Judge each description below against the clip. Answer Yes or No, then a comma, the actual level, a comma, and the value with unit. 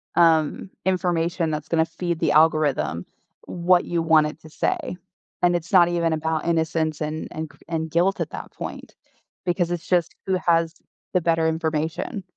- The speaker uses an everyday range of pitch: No, narrow, 1.6 semitones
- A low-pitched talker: No, medium, 165 Hz